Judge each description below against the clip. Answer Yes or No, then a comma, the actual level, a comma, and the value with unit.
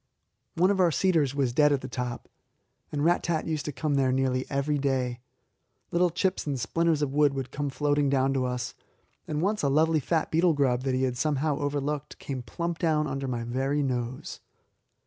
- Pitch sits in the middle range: Yes, medium, 145 Hz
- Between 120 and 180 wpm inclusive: No, average, 200 wpm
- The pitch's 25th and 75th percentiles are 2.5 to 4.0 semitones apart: Yes, average, 3.0 semitones